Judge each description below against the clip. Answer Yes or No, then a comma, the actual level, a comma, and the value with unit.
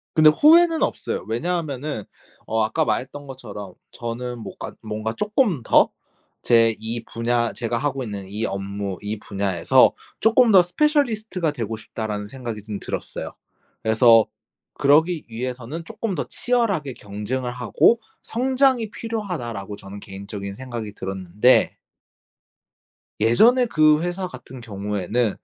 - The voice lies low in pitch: Yes, low, 120 Hz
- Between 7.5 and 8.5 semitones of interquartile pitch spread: Yes, wide, 8.1 semitones